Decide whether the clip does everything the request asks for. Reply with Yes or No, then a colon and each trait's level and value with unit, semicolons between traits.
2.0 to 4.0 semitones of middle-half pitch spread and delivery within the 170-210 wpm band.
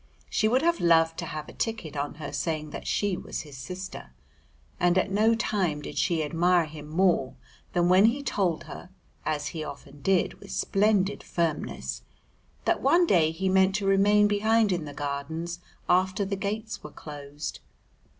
No: average, 4.7 semitones; average, 175 wpm